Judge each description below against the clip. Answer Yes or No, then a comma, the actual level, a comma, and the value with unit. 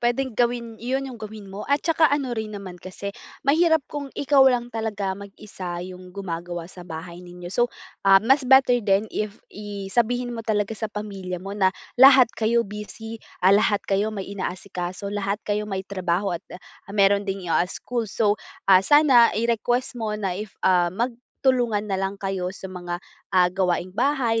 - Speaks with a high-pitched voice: Yes, high, 205 Hz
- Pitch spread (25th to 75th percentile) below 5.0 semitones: Yes, average, 4.0 semitones